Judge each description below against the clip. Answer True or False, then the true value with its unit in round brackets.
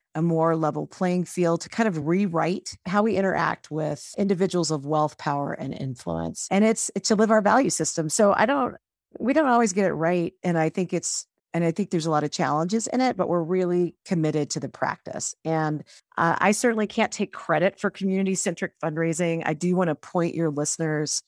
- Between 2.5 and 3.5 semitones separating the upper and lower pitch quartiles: False (3.9 semitones)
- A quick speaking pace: True (210 wpm)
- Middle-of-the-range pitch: True (175 Hz)